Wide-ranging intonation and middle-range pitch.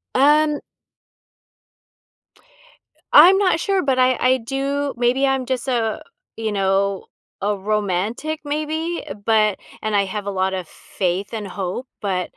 No: wide, 6.1 semitones; high, 230 Hz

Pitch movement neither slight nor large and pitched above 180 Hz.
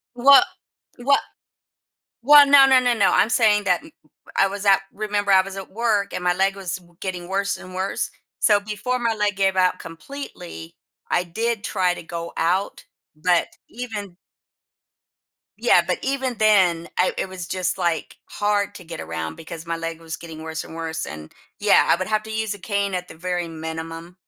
Yes: average, 3.9 semitones; high, 190 Hz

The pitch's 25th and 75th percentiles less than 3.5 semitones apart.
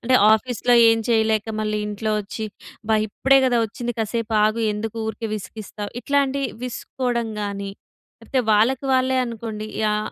Yes: narrow, 2.6 semitones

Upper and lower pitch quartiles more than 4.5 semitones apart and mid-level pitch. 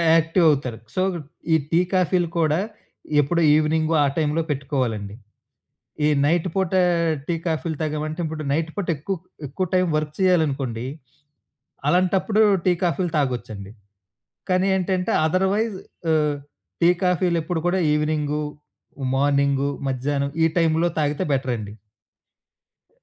No: average, 3.8 semitones; medium, 155 Hz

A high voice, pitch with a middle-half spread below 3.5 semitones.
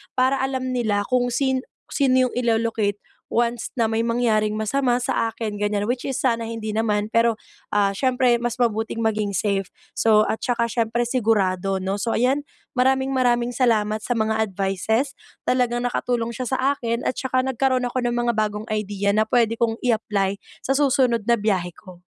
Yes: high, 230 Hz; average, 2.9 semitones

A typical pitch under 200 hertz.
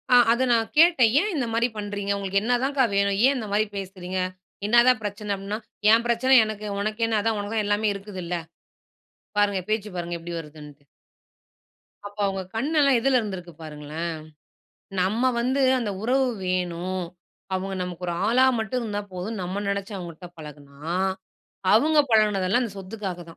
No: high, 205 Hz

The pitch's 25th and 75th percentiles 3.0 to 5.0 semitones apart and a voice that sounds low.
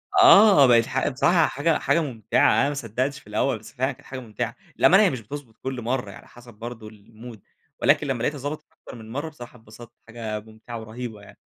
Yes: average, 4.1 semitones; low, 120 Hz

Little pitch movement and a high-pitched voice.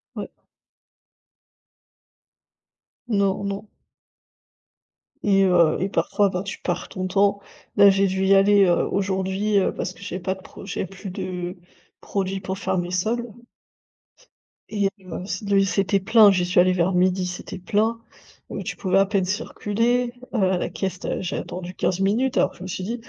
Yes: narrow, 1.6 semitones; high, 195 Hz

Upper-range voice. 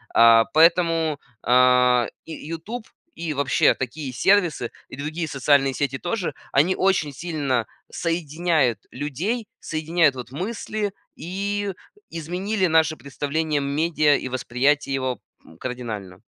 No: medium, 150 Hz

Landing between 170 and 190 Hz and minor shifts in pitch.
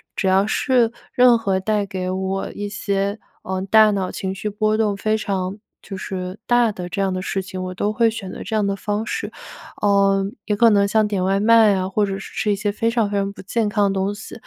No: high, 200 Hz; narrow, 1.9 semitones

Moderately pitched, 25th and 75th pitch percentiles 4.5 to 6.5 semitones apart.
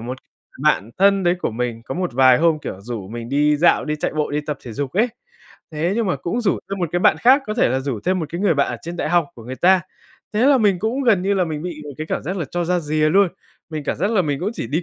Yes: medium, 165 Hz; average, 5.2 semitones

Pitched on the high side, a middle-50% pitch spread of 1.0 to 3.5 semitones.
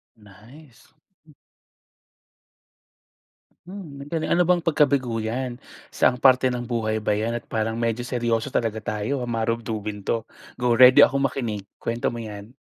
No: low, 120 Hz; average, 2.9 semitones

